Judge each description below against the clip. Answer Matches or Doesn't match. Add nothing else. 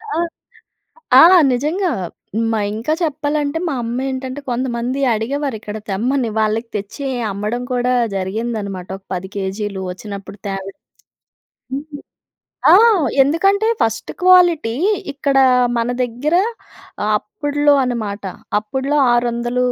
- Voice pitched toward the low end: Doesn't match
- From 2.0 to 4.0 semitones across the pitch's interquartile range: Doesn't match